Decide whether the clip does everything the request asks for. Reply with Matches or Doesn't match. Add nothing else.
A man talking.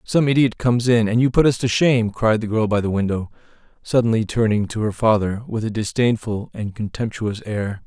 Matches